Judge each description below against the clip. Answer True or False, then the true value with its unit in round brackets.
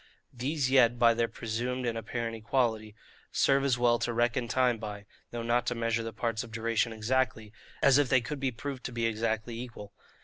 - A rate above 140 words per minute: True (200 wpm)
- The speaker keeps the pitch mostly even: True (1.9 semitones)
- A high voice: False (120 Hz)